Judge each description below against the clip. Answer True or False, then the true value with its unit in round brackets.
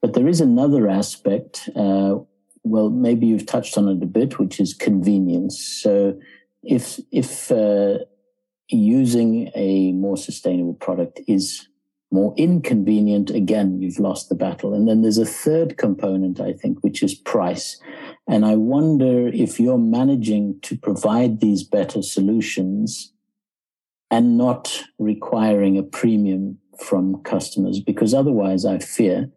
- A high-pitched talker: False (105 Hz)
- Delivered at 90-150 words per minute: True (135 wpm)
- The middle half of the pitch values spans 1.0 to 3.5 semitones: False (4.3 semitones)